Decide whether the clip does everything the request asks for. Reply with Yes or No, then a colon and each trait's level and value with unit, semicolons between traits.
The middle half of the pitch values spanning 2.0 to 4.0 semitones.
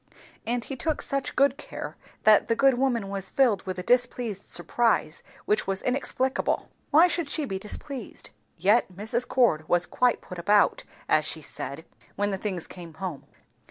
No: average, 5.3 semitones